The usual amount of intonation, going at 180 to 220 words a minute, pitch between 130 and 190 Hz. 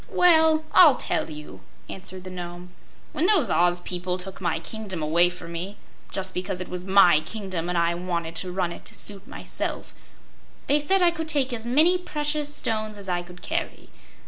No: wide, 8.2 semitones; average, 190 wpm; medium, 185 Hz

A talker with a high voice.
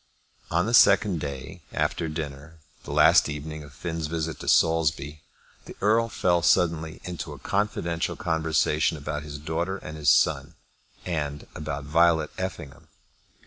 No: very low, 80 Hz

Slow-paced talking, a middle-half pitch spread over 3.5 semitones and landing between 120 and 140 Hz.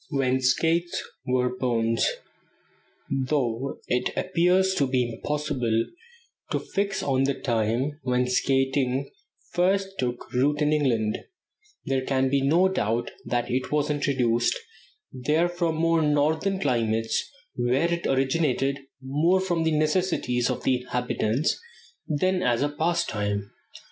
Yes: slow, 125 wpm; average, 4.3 semitones; low, 135 Hz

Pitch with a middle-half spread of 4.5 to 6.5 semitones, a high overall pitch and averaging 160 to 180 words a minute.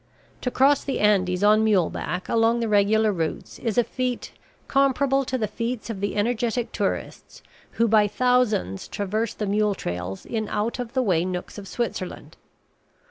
No: average, 3.3 semitones; high, 220 Hz; average, 170 wpm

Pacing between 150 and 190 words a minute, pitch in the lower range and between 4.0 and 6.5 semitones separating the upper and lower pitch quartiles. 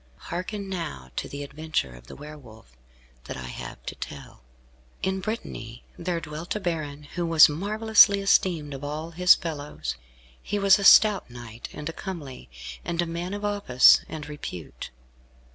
No: average, 165 wpm; medium, 160 Hz; average, 5.2 semitones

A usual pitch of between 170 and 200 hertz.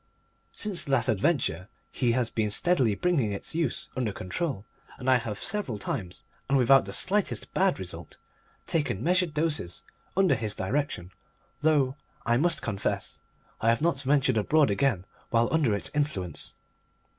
No: low, 130 Hz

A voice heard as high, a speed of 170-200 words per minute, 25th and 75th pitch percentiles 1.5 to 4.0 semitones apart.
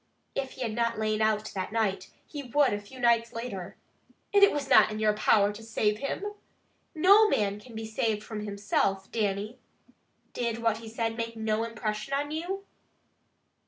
Yes: high, 225 Hz; average, 175 wpm; narrow, 2.6 semitones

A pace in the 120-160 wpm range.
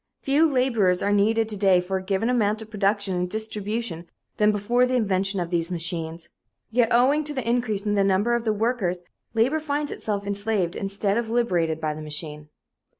No: average, 195 wpm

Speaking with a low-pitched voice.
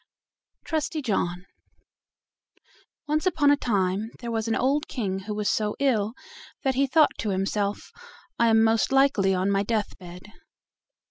No: high, 220 Hz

